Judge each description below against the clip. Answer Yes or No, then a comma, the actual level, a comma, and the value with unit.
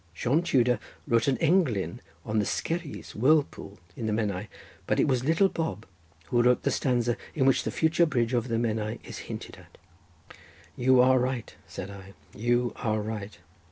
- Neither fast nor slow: Yes, average, 175 wpm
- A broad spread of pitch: No, average, 3.8 semitones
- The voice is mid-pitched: No, low, 120 Hz